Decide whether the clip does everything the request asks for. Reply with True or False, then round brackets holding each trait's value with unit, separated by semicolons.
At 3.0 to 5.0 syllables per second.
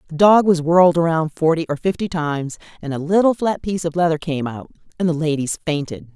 False (6.0 syllables/s)